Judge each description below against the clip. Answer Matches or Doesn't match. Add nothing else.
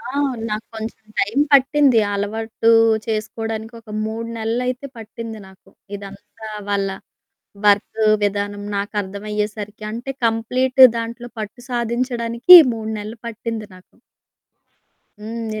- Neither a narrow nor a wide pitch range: Doesn't match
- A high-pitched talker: Matches